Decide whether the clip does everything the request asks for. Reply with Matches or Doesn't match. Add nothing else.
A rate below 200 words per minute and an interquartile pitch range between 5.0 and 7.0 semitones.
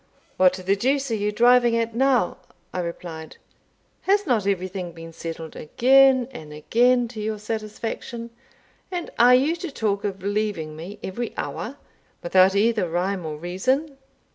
Matches